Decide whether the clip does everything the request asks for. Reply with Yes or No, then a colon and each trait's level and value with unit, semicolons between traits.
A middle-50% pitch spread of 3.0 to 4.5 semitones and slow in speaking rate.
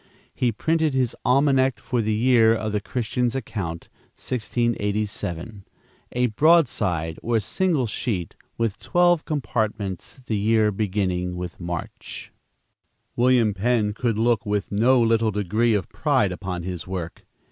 Yes: average, 3.9 semitones; slow, 130 wpm